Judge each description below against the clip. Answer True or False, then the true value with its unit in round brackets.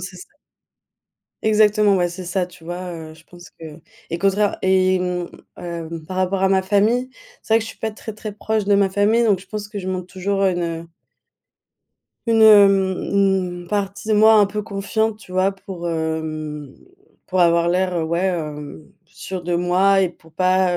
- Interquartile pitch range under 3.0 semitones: True (2.6 semitones)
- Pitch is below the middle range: False (185 Hz)